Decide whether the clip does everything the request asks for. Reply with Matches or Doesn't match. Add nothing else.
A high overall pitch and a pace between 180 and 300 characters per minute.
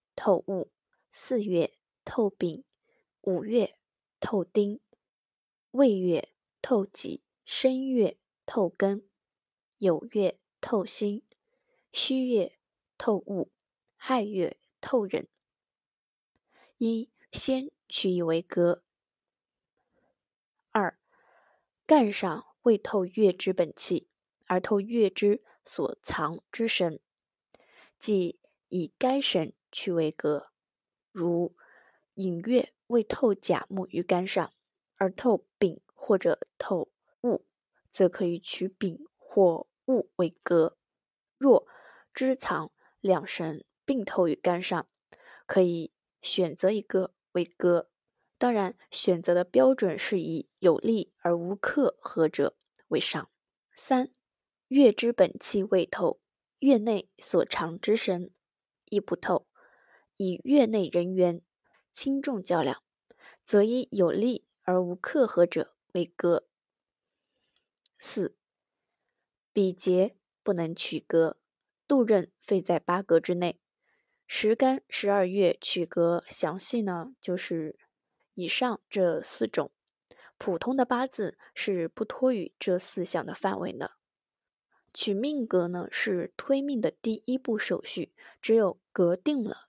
Doesn't match